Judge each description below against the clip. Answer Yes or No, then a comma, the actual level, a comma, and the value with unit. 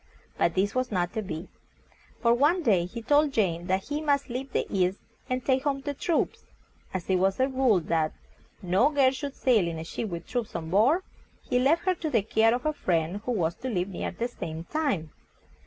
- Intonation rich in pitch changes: Yes, wide, 7.1 semitones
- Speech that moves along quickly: Yes, fast, 220 wpm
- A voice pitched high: Yes, high, 230 Hz